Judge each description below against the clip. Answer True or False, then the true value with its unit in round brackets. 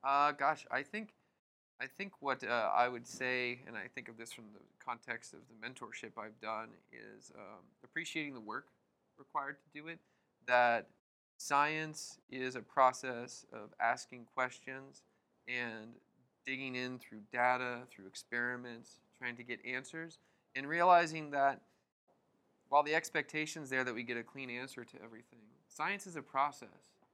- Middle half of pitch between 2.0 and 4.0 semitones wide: True (3.3 semitones)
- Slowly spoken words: False (160 wpm)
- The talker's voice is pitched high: False (130 Hz)